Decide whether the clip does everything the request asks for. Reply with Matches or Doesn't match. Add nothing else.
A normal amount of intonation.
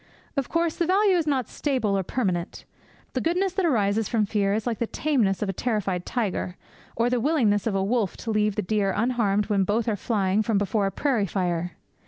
Matches